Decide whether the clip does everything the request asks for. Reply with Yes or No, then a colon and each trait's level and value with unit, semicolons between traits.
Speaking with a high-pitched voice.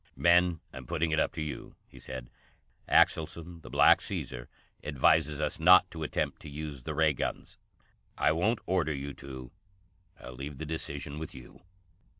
No: very low, 75 Hz